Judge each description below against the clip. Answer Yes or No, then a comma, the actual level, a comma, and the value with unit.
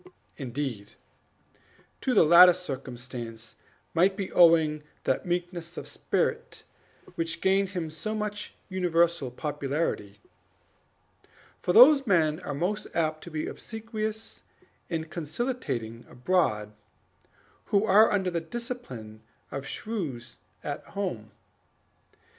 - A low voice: No, medium, 170 Hz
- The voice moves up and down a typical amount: No, wide, 6.3 semitones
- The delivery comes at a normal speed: No, slow, 105 wpm